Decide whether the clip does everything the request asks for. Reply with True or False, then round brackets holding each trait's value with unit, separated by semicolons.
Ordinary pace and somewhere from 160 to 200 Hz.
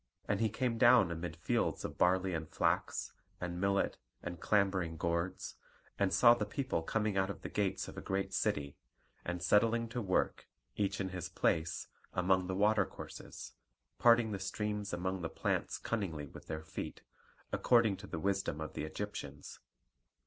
False (170 wpm; 95 Hz)